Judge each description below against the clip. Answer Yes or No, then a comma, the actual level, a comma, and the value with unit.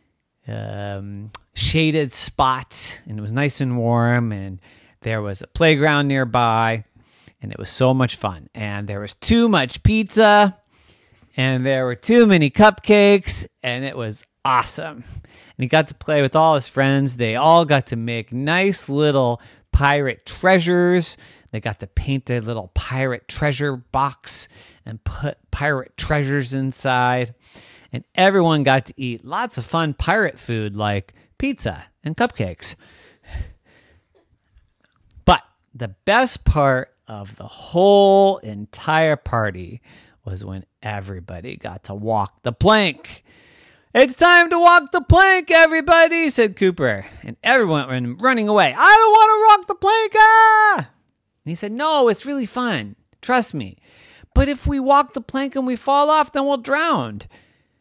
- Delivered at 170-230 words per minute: No, average, 150 wpm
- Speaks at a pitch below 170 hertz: Yes, low, 135 Hz